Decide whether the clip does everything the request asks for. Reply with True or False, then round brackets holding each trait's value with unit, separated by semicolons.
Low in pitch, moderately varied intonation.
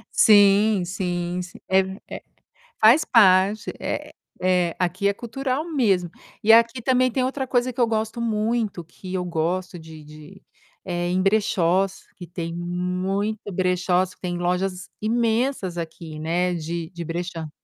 False (185 Hz; 3.9 semitones)